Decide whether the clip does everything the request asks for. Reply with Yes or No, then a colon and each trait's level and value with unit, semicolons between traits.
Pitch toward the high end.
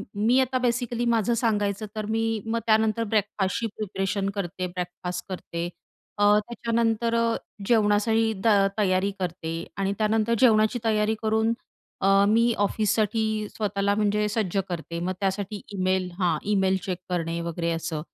Yes: high, 205 Hz